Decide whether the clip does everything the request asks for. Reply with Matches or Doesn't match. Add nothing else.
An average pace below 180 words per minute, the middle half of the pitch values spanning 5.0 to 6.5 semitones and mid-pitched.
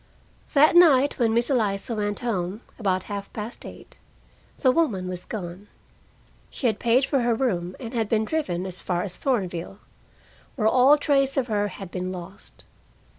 Doesn't match